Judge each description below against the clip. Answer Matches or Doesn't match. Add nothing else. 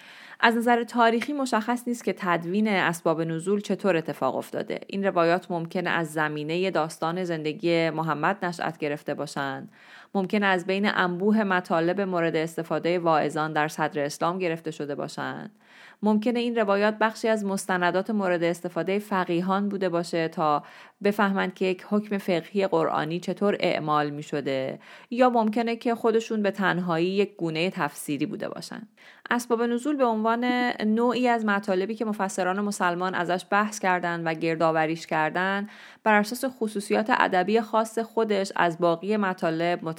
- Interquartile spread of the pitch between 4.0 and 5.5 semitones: Matches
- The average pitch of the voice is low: Doesn't match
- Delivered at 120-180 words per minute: Matches